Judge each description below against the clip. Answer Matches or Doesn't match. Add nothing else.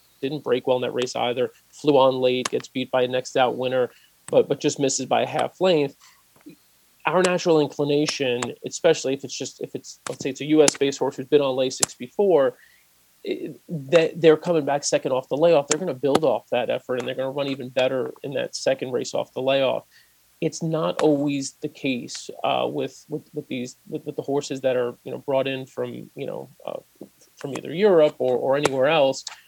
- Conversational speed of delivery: Doesn't match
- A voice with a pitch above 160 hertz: Doesn't match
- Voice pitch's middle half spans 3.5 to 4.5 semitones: Doesn't match